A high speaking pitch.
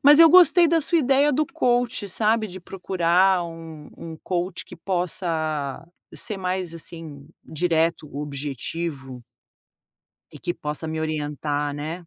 No: medium, 170 Hz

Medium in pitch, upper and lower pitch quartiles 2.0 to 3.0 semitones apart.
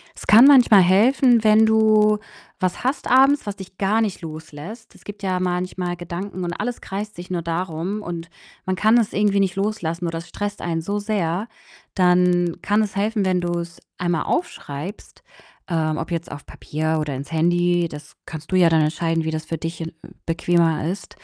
No: medium, 180 Hz; average, 3.9 semitones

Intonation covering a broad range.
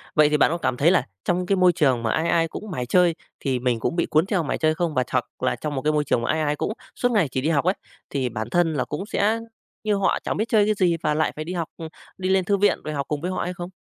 No: average, 3.7 semitones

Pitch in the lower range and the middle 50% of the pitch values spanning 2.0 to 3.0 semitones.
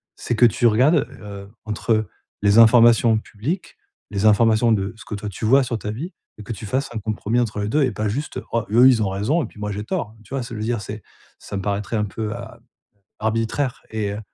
Yes: low, 110 Hz; narrow, 2.4 semitones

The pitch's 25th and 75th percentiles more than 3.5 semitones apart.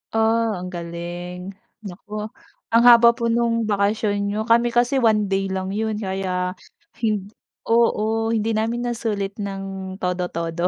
No: average, 3.2 semitones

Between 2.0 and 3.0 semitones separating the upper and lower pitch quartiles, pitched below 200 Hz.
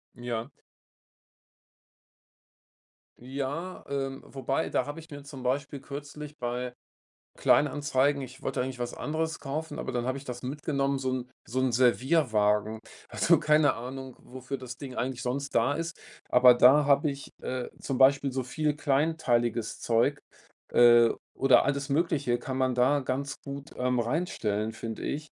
Yes: narrow, 2.5 semitones; low, 135 Hz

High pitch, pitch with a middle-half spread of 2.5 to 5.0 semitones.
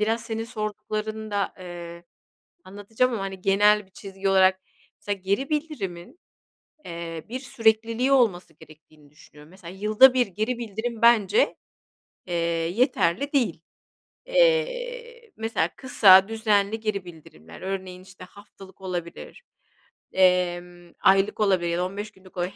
Yes: high, 200 Hz; average, 3.9 semitones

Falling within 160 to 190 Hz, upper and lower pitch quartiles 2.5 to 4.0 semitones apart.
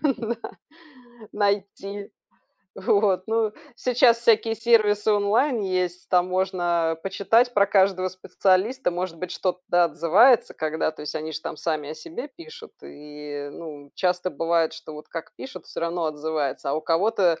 No: medium, 185 Hz; average, 4.5 semitones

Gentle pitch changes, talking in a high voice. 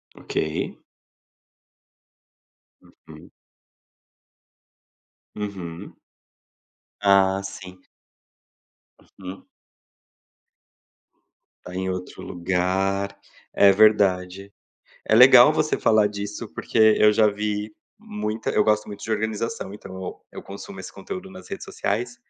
No: narrow, 2.3 semitones; low, 105 Hz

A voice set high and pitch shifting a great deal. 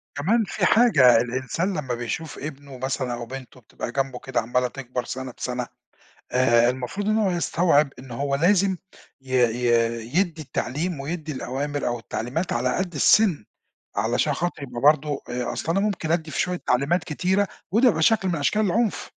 No: medium, 140 Hz; wide, 5.9 semitones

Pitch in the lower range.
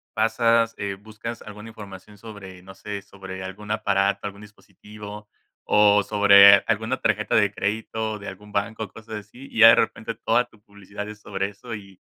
Yes: low, 105 Hz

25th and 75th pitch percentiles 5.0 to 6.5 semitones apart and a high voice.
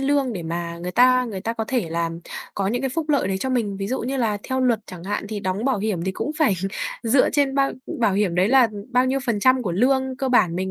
Yes: wide, 5.4 semitones; high, 230 Hz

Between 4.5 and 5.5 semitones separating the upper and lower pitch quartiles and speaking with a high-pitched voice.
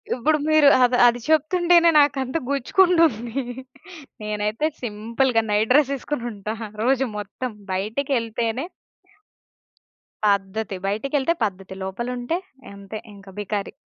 Yes: average, 5.1 semitones; high, 240 Hz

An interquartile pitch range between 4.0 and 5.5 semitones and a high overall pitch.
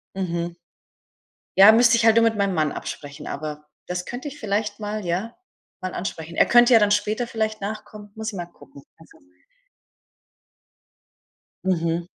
Yes: average, 4.3 semitones; high, 205 Hz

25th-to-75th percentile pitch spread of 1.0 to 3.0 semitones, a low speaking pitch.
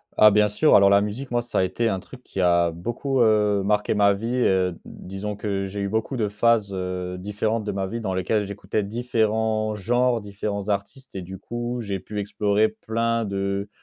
Yes: narrow, 2.5 semitones; low, 105 Hz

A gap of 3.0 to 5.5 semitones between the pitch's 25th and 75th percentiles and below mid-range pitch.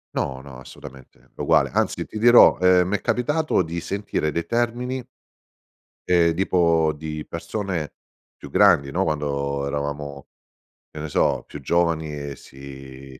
Yes: average, 4.6 semitones; very low, 80 Hz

